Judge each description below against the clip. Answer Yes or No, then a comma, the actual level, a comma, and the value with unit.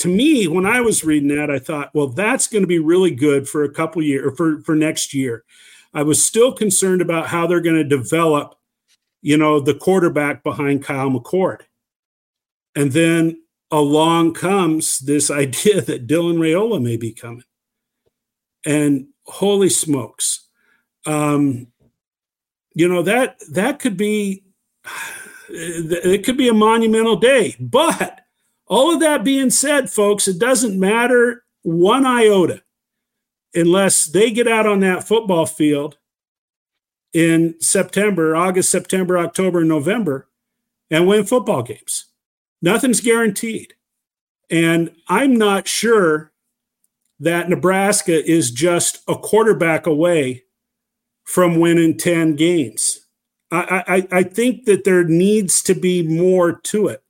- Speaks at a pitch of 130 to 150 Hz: No, medium, 175 Hz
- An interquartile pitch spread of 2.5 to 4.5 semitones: No, wide, 5.5 semitones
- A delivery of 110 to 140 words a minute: Yes, slow, 135 wpm